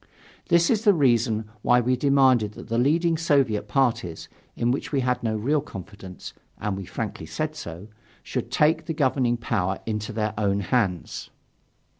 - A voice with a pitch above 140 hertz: No, low, 120 Hz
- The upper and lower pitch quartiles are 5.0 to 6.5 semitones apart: Yes, average, 5.3 semitones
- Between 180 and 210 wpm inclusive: No, average, 165 wpm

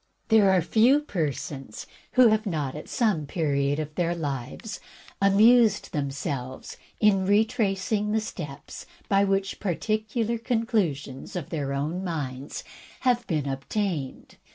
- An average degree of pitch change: No, wide, 7.1 semitones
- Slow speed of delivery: Yes, slow, 130 wpm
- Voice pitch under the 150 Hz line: No, medium, 185 Hz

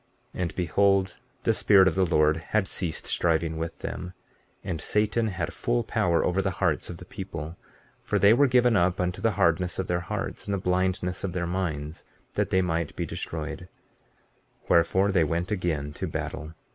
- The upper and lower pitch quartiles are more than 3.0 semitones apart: No, narrow, 2.6 semitones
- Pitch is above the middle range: No, very low, 90 Hz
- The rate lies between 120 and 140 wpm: No, average, 185 wpm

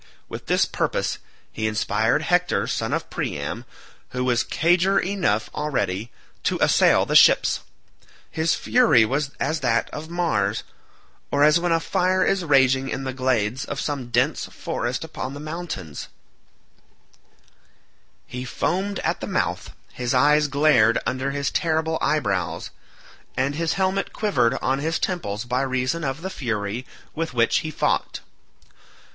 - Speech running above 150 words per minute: No, average, 145 wpm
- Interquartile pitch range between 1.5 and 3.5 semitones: No, average, 5.2 semitones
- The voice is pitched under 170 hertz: Yes, medium, 140 Hz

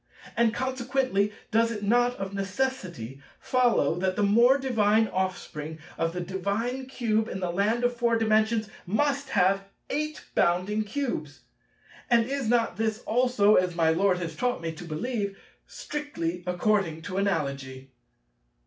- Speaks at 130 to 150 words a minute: Yes, average, 145 wpm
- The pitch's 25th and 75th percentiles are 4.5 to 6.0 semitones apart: Yes, average, 5.2 semitones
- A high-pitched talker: Yes, high, 210 Hz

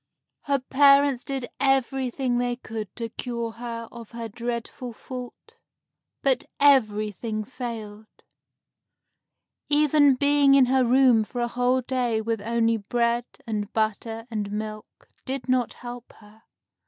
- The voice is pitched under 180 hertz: No, high, 240 Hz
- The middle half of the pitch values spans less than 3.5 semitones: Yes, average, 2.7 semitones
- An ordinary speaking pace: No, slow, 130 wpm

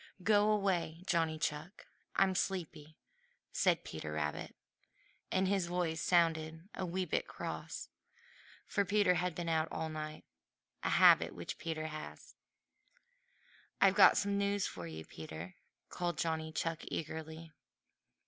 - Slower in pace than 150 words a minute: Yes, slow, 135 wpm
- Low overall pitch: No, medium, 165 Hz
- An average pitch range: Yes, average, 3.0 semitones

